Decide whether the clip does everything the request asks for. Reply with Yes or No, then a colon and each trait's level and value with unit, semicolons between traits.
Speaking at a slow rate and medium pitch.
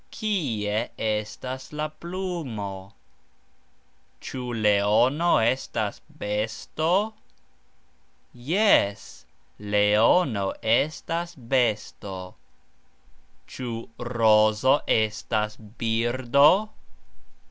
No: slow, 55 wpm; low, 115 Hz